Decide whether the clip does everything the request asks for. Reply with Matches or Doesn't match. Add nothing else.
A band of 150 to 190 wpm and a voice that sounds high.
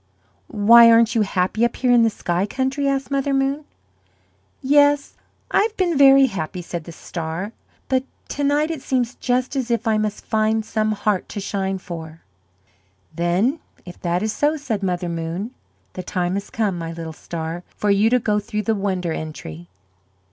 Matches